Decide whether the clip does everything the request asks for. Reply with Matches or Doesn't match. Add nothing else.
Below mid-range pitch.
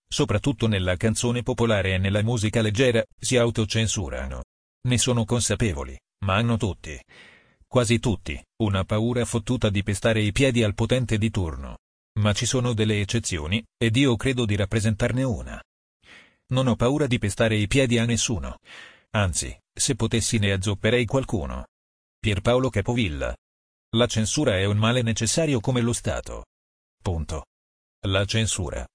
Matches